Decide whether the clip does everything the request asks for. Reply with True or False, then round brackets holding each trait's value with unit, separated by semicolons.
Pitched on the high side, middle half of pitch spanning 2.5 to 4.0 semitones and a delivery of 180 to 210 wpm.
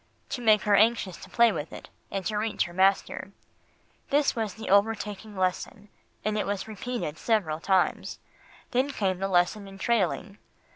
False (205 Hz; 2.8 semitones; 165 wpm)